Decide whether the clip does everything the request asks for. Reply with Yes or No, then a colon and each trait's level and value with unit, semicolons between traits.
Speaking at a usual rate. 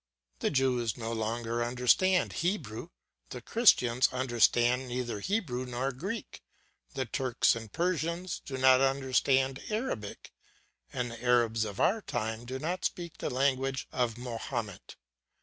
No: slow, 130 wpm